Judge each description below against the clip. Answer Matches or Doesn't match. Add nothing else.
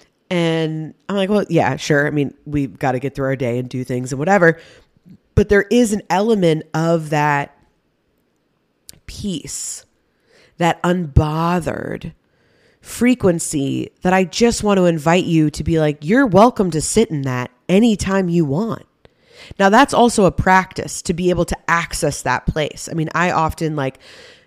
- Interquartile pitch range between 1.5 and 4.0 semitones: Doesn't match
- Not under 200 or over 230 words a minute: Doesn't match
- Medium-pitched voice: Matches